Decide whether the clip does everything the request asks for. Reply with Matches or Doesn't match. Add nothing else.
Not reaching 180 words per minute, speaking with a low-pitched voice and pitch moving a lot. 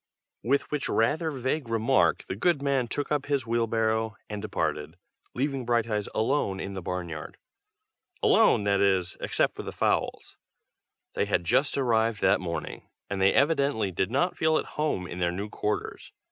Matches